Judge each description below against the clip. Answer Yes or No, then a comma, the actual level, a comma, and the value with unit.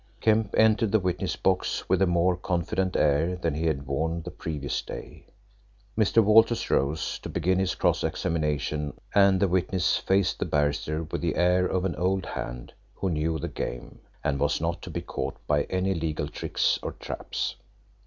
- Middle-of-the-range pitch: No, very low, 85 Hz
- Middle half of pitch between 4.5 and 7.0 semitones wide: No, average, 3.7 semitones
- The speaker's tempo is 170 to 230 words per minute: Yes, average, 180 wpm